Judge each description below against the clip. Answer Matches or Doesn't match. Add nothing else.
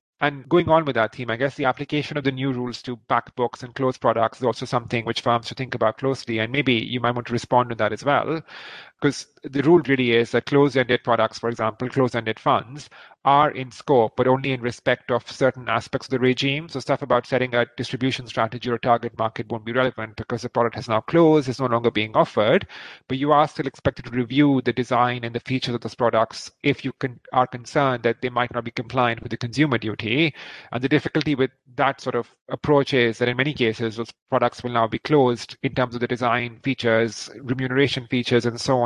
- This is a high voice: Doesn't match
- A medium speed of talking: Doesn't match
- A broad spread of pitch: Doesn't match